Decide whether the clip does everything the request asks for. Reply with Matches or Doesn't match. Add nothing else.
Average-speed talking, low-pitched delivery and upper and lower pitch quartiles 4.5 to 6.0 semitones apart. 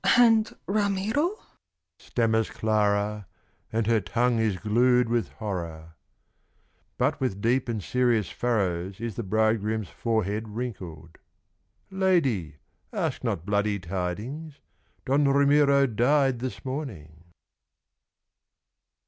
Doesn't match